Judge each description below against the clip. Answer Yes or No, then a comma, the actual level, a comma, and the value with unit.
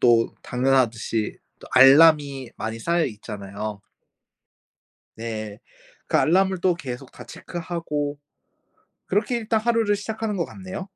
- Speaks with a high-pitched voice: No, medium, 145 Hz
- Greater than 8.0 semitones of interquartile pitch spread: Yes, wide, 8.4 semitones